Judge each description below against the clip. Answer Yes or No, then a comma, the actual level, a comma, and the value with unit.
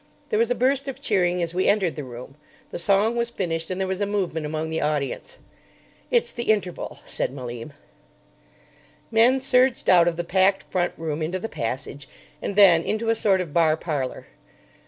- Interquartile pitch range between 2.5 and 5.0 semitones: No, wide, 5.4 semitones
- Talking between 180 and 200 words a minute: Yes, average, 190 wpm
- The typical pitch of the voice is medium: Yes, medium, 180 Hz